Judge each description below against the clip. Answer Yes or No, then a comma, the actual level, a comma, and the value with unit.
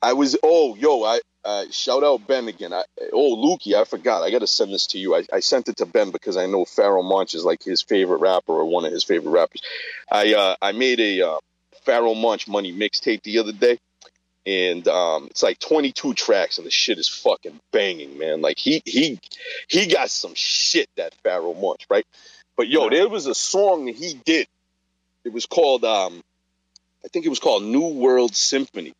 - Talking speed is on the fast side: Yes, fast, 210 wpm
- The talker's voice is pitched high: Yes, very high, 355 Hz